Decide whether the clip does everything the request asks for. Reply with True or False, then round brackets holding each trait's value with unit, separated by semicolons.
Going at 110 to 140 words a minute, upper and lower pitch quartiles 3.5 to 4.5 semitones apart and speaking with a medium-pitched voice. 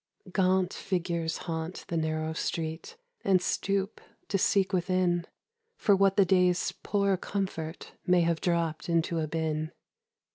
False (135 wpm; 2.8 semitones; 175 Hz)